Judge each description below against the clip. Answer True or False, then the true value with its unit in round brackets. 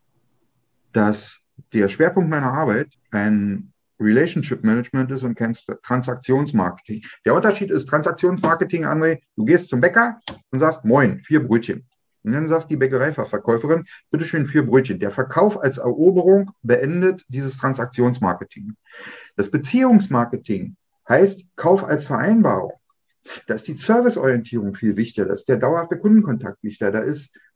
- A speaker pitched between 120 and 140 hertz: True (135 Hz)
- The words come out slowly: False (135 wpm)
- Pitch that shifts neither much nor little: False (6.7 semitones)